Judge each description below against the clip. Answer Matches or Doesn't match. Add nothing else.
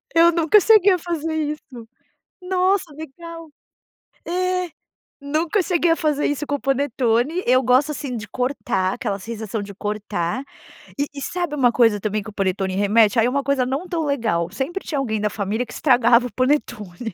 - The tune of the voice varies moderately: Doesn't match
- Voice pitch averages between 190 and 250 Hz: Doesn't match